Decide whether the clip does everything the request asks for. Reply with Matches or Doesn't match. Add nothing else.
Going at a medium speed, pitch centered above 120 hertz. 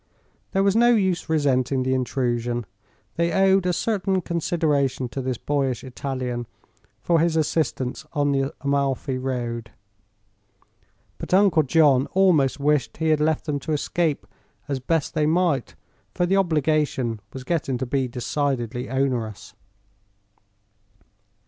Doesn't match